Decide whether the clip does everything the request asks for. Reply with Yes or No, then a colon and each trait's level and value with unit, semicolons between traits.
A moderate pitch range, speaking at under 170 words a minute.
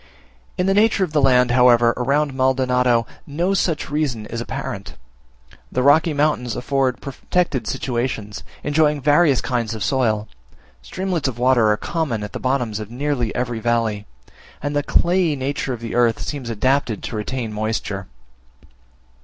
Yes: average, 3.9 semitones; average, 155 wpm